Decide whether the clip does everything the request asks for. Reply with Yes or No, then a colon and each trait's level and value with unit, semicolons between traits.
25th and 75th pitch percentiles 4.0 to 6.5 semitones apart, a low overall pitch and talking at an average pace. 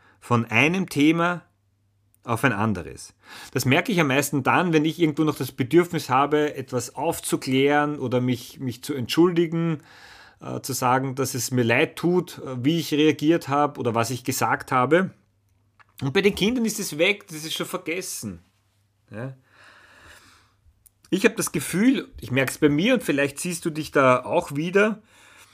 No: average, 5.1 semitones; medium, 145 Hz; average, 170 wpm